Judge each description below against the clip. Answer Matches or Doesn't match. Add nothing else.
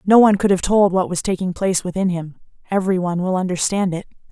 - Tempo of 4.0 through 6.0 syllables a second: Doesn't match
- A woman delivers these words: Matches